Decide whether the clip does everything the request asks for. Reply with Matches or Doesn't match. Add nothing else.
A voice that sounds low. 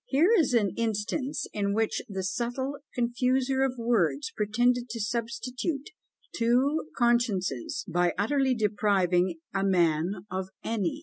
Doesn't match